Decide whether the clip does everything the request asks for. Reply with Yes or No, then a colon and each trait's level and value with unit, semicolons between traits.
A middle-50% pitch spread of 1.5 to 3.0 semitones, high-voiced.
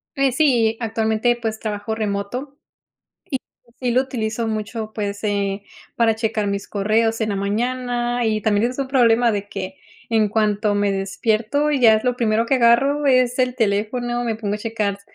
Yes: average, 2.7 semitones; high, 225 Hz